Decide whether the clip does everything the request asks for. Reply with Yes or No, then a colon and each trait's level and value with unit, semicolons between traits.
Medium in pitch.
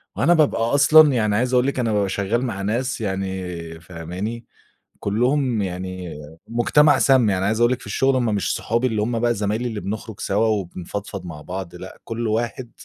No: low, 110 Hz